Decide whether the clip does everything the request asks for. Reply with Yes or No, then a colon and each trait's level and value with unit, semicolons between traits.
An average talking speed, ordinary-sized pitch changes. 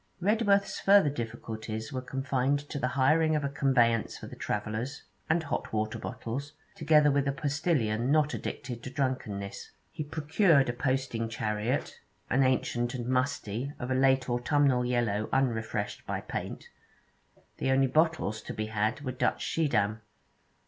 Yes: average, 150 wpm; average, 4.1 semitones